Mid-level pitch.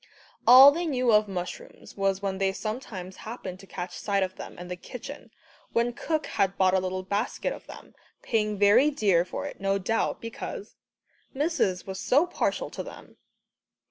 No: high, 205 Hz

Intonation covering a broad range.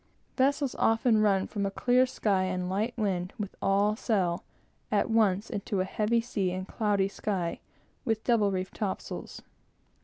No: average, 2.9 semitones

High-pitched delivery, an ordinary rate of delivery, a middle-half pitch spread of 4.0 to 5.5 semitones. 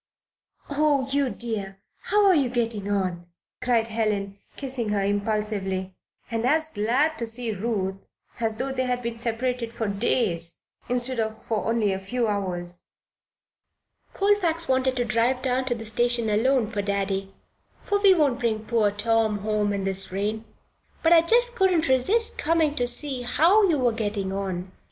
Yes: high, 230 Hz; average, 165 wpm; average, 4.3 semitones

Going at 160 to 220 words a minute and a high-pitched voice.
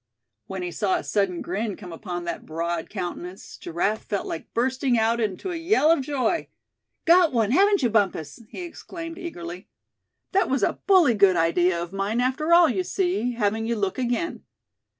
Yes: average, 180 wpm; high, 225 Hz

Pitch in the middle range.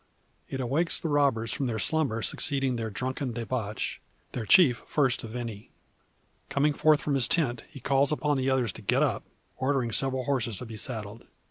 No: low, 130 Hz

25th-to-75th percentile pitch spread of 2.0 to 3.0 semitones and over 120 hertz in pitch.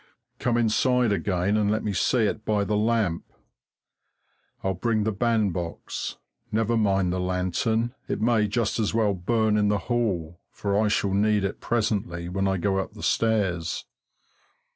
No: narrow, 2.6 semitones; low, 105 Hz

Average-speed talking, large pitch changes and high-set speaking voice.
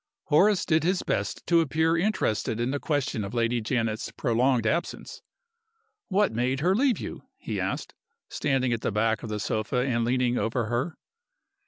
No: average, 170 wpm; wide, 5.9 semitones; low, 125 Hz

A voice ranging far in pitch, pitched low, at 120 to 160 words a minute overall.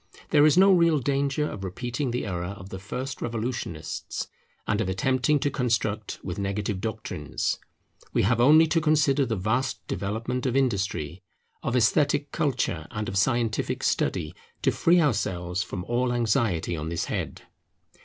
Yes: wide, 5.8 semitones; low, 115 Hz; average, 155 wpm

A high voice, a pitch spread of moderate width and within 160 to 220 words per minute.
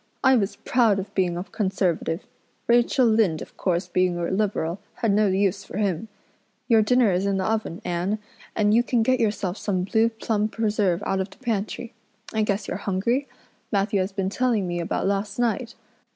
Yes: high, 205 Hz; average, 3.0 semitones; average, 190 wpm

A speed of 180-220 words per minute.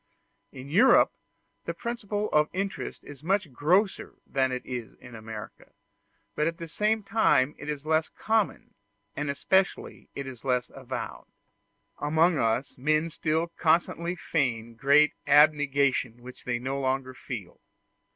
No: average, 140 wpm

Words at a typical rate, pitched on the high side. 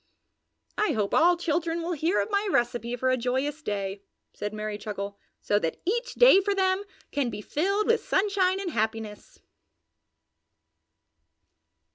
Yes: average, 145 wpm; very high, 295 Hz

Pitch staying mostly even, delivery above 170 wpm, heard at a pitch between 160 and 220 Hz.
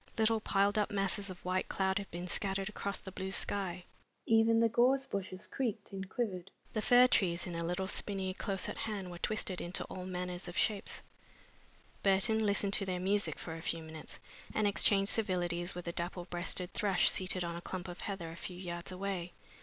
Yes: narrow, 2.3 semitones; average, 200 wpm; high, 190 Hz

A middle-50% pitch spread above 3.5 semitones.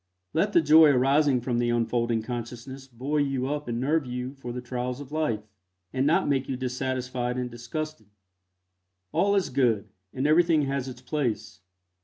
No: average, 3.2 semitones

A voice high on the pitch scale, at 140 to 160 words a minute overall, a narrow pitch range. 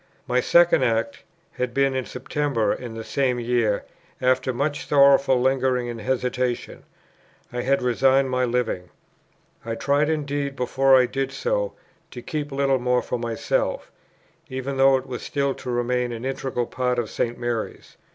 No: low, 130 Hz; average, 155 wpm; narrow, 2.1 semitones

